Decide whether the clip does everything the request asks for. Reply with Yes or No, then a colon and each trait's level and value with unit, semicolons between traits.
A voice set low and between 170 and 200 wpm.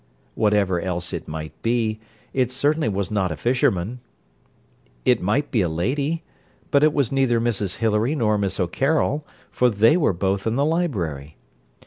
No: low, 110 Hz; average, 160 wpm